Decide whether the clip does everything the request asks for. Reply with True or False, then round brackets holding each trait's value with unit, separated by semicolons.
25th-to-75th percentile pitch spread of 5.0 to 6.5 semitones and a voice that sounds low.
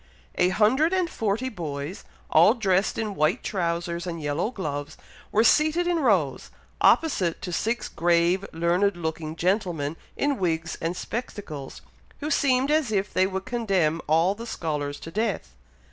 False (5.6 semitones; 185 Hz)